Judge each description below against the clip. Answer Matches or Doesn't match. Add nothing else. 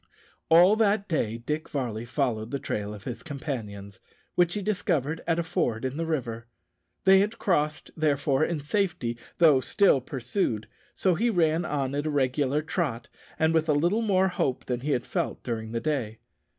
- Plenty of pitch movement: Matches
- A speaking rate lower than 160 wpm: Doesn't match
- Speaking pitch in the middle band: Matches